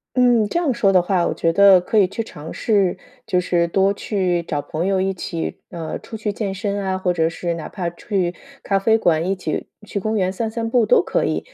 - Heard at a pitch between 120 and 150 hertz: No, high, 190 Hz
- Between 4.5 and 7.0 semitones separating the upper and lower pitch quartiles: No, average, 3.4 semitones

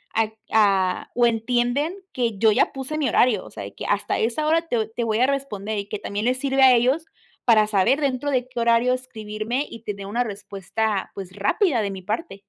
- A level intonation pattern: No, average, 3.8 semitones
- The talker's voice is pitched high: Yes, high, 230 Hz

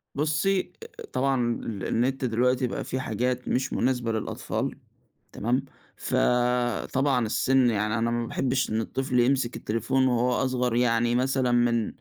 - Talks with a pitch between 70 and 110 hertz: No, low, 125 Hz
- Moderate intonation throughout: No, narrow, 1.9 semitones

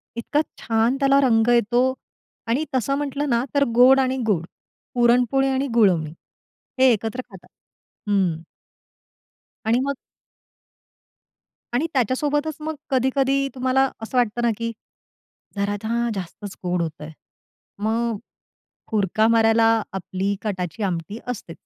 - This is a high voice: Yes, high, 235 Hz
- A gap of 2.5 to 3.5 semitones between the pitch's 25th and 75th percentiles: No, average, 4.3 semitones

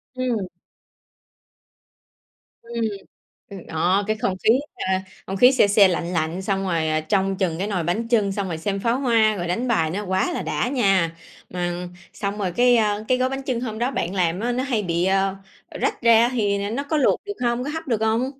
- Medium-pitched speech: No, high, 205 Hz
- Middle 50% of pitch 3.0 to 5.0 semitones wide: Yes, average, 4.3 semitones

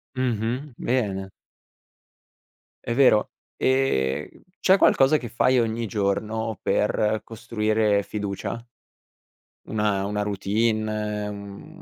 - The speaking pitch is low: Yes, low, 110 Hz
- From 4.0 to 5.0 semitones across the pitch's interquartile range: No, narrow, 2.4 semitones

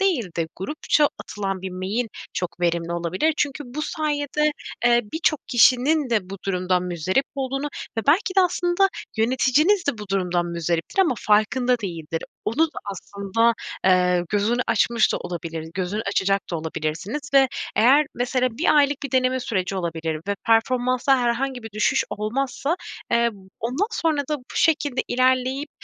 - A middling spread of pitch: No, wide, 6.8 semitones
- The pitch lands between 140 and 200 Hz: No, high, 235 Hz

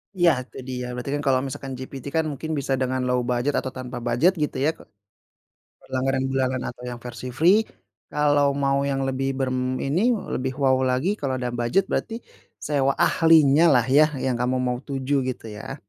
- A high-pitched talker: No, low, 135 Hz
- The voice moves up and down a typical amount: No, narrow, 2.1 semitones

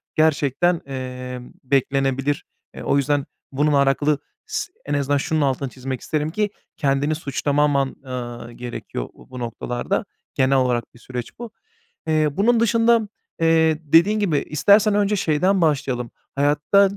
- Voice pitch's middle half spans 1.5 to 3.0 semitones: No, average, 3.7 semitones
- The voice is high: No, medium, 145 Hz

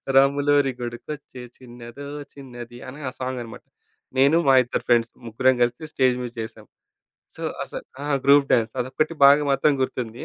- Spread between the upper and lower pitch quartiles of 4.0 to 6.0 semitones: No, narrow, 2.6 semitones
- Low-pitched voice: Yes, low, 130 Hz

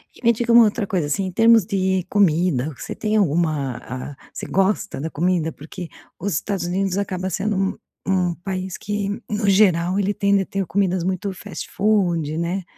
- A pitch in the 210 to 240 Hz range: No, high, 190 Hz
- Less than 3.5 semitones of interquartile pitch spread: Yes, average, 2.9 semitones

